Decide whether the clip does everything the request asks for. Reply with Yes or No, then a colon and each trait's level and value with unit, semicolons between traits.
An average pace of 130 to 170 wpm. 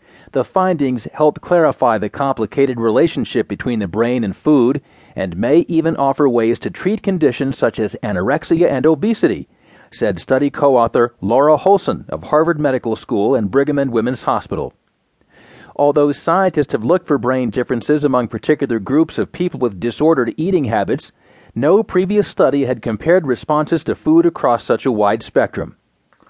Yes: average, 155 wpm